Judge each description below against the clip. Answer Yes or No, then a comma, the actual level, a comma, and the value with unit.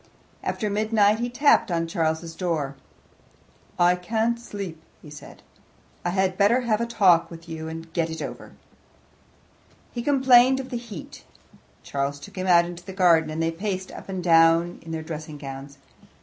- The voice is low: No, medium, 175 Hz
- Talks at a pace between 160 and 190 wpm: Yes, average, 170 wpm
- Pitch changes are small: No, average, 4.7 semitones